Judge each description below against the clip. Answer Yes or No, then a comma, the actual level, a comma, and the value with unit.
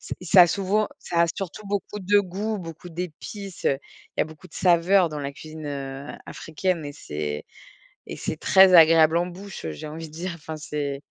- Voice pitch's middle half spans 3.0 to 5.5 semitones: Yes, average, 3.9 semitones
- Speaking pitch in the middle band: Yes, medium, 165 Hz